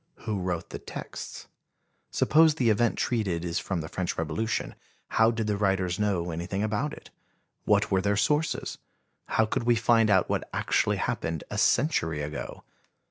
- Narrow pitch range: No, average, 4.5 semitones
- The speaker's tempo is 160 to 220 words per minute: Yes, average, 165 wpm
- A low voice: Yes, low, 105 Hz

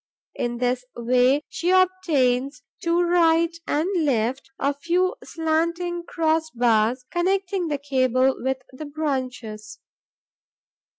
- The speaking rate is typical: No, slow, 110 wpm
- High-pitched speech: Yes, very high, 285 Hz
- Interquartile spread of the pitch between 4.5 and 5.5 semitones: Yes, average, 5.1 semitones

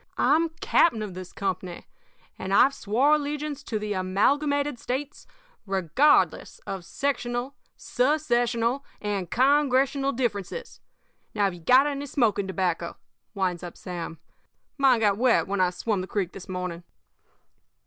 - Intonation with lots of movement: Yes, wide, 6.7 semitones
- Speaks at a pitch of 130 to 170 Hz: No, high, 225 Hz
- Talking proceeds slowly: Yes, slow, 130 wpm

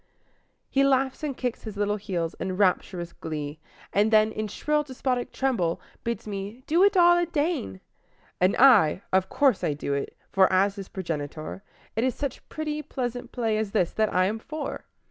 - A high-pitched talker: Yes, high, 215 Hz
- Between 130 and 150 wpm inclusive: No, average, 180 wpm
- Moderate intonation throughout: No, wide, 6.3 semitones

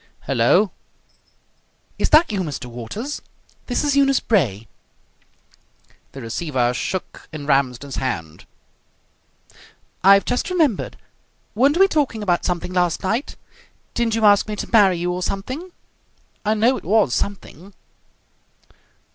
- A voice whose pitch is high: Yes, high, 195 Hz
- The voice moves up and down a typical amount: No, wide, 8.5 semitones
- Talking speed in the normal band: No, slow, 125 wpm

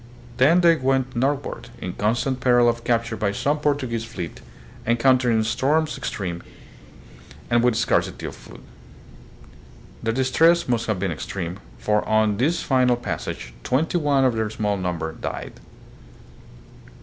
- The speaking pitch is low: Yes, low, 120 Hz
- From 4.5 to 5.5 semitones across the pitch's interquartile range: No, average, 3.6 semitones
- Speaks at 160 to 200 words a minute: No, slow, 135 wpm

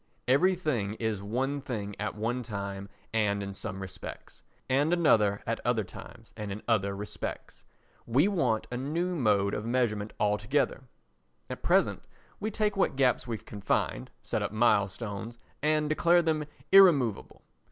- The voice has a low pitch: Yes, low, 115 Hz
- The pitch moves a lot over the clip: Yes, wide, 6.3 semitones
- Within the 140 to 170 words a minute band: Yes, average, 150 wpm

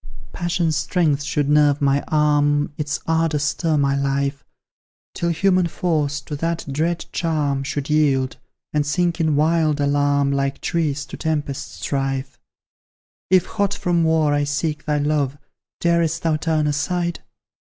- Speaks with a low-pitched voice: No, medium, 150 Hz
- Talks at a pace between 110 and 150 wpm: Yes, average, 140 wpm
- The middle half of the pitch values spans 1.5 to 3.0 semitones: Yes, narrow, 2.4 semitones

